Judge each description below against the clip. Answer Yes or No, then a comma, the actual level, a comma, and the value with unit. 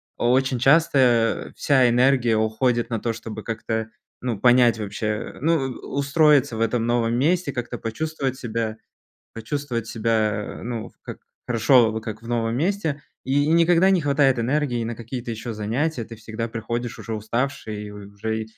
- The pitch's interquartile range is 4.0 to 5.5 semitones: No, average, 3.4 semitones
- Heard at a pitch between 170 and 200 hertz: No, low, 120 Hz